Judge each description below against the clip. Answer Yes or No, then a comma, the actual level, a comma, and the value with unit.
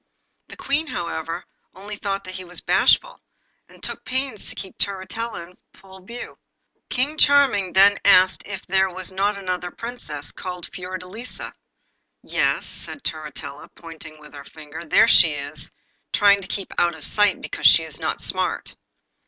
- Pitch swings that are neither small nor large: Yes, average, 3.3 semitones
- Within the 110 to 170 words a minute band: Yes, average, 160 wpm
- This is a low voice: No, high, 190 Hz